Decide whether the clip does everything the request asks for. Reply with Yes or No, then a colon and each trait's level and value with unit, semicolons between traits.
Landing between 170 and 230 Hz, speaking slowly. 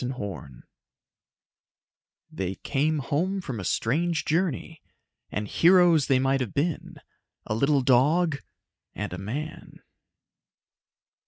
No: medium, 140 Hz; slow, 105 wpm